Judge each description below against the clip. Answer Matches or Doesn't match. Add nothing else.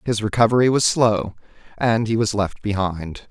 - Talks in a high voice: Doesn't match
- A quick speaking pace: Doesn't match